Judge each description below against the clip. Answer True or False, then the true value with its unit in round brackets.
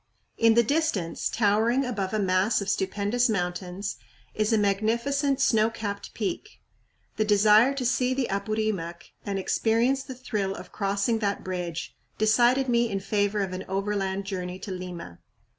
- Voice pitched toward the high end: True (210 Hz)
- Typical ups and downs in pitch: True (3.4 semitones)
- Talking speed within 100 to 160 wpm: True (155 wpm)